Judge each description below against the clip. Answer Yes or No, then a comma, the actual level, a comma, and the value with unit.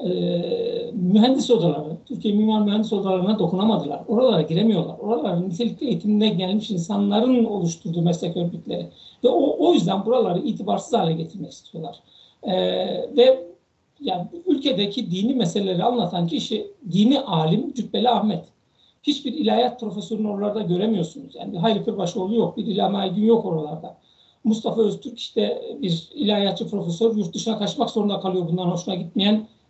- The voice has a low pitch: No, high, 210 Hz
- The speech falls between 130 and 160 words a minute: Yes, average, 135 wpm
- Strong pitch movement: No, average, 4.2 semitones